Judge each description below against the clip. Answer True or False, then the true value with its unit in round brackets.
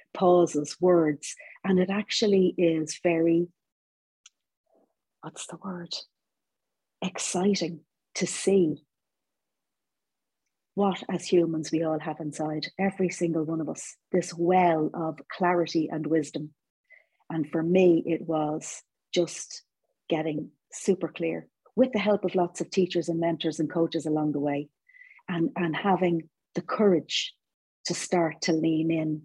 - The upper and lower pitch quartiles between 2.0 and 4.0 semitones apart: True (2.4 semitones)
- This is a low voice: False (170 Hz)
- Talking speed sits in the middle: False (130 wpm)